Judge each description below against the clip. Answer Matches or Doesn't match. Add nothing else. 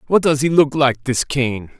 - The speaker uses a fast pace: Matches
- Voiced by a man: Matches